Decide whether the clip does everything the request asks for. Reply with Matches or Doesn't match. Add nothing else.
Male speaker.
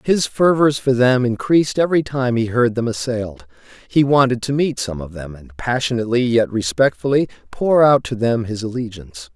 Matches